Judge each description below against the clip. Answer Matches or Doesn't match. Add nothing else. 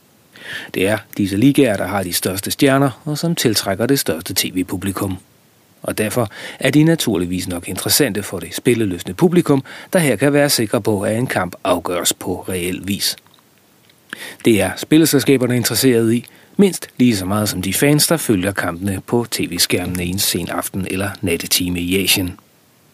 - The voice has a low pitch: Matches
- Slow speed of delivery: Doesn't match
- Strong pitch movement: Matches